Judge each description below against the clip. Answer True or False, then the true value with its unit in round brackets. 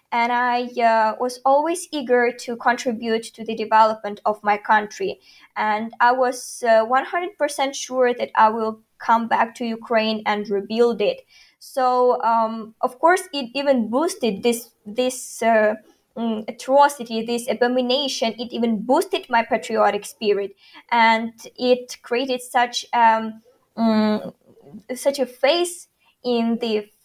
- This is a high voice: True (240 Hz)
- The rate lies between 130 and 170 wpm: True (140 wpm)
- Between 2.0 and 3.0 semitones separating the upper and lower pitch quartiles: True (2.4 semitones)